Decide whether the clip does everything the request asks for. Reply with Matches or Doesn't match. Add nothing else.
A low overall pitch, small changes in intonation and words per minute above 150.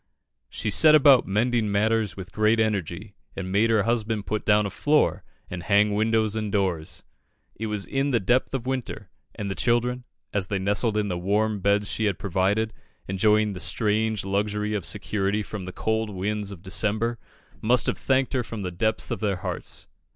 Matches